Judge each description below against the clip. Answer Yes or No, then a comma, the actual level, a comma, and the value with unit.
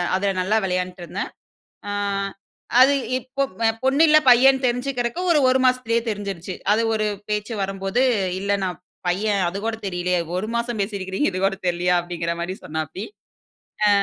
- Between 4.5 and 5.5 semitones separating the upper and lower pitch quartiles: Yes, average, 4.9 semitones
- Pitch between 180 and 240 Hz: Yes, high, 200 Hz